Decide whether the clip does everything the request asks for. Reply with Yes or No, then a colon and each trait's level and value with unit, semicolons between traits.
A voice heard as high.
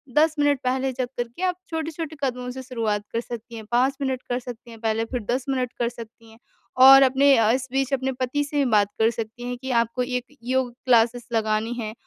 Yes: very high, 250 Hz